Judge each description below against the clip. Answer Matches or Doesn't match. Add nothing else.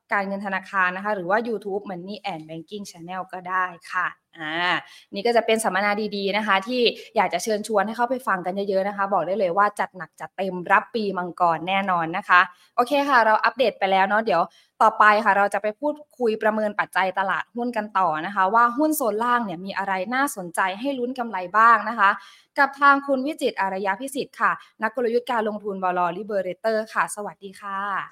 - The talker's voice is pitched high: Matches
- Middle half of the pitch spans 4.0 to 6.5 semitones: Doesn't match